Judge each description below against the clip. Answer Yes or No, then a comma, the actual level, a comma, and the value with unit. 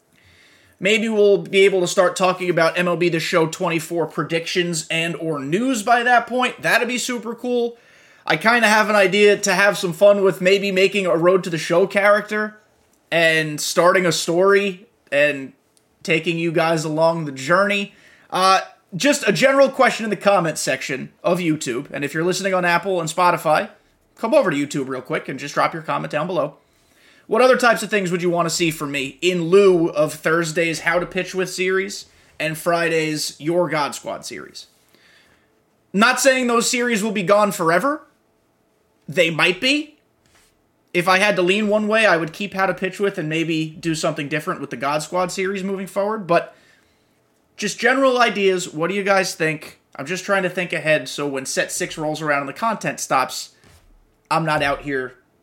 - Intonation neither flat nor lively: Yes, average, 3.9 semitones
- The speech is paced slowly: No, average, 190 wpm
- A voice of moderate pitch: Yes, medium, 180 Hz